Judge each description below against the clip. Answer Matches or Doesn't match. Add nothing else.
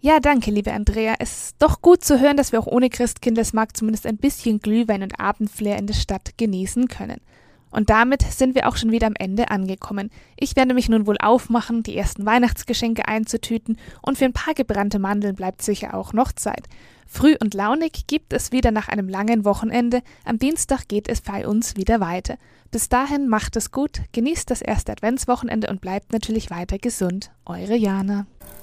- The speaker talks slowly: Doesn't match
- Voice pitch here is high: Matches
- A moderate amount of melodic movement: Matches